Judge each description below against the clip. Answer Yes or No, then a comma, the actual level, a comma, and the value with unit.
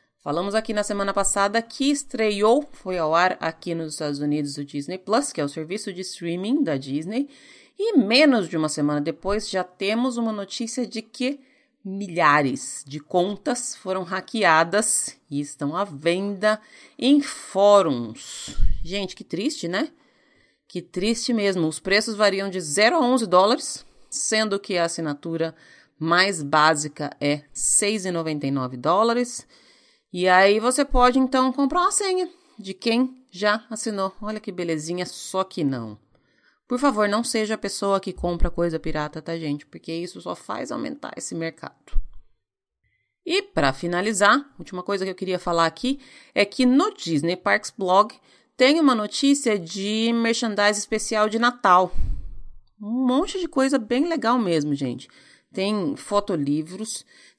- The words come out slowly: No, average, 150 wpm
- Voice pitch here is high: Yes, high, 200 Hz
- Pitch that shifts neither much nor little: No, wide, 6.2 semitones